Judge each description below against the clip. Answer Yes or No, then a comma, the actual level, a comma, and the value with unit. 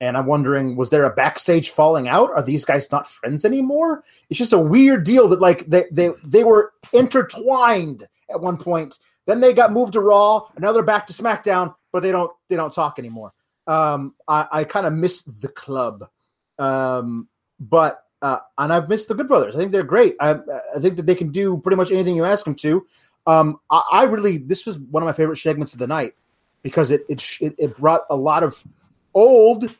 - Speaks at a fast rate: Yes, fast, 215 wpm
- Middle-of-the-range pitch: Yes, medium, 175 Hz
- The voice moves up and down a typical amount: No, wide, 6.0 semitones